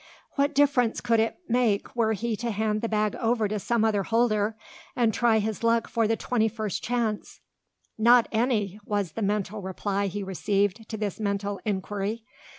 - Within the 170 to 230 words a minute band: Yes, average, 175 wpm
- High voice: Yes, high, 220 Hz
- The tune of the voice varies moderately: No, narrow, 2.2 semitones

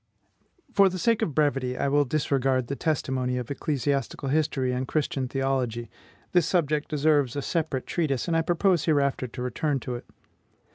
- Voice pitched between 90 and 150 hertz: Yes, medium, 140 Hz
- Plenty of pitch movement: No, average, 3.2 semitones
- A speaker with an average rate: Yes, average, 165 wpm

